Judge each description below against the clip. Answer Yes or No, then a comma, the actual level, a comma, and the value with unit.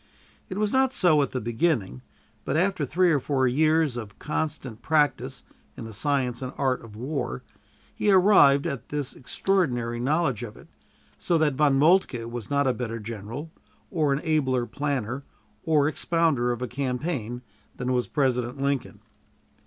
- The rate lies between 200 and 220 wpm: No, average, 160 wpm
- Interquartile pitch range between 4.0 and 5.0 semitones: Yes, average, 4.4 semitones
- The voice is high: No, medium, 140 Hz